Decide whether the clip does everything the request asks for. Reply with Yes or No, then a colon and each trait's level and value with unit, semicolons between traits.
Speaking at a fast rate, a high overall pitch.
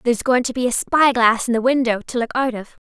Yes: fast, 290 wpm; high, 245 Hz